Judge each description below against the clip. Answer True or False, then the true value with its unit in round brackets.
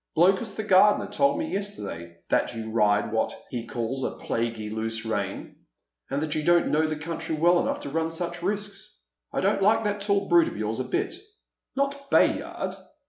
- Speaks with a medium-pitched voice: True (170 Hz)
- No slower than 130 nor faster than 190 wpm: False (205 wpm)